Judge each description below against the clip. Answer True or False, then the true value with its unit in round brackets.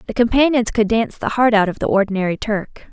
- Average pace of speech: False (225 wpm)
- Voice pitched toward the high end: True (220 Hz)